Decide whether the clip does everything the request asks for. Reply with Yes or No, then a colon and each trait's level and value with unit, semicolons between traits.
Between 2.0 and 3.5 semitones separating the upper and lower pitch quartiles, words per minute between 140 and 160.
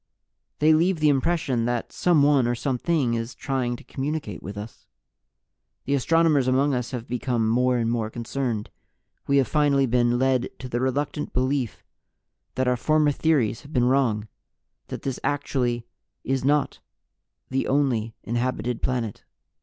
Yes: average, 3.1 semitones; average, 150 wpm